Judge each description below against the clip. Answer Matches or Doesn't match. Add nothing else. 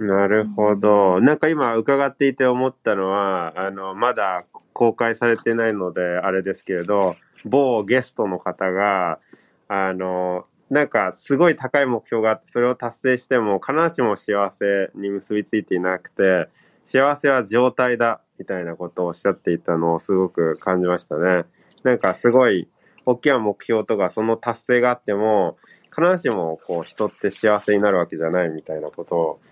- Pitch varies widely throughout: Doesn't match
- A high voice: Doesn't match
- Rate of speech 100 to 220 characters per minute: Doesn't match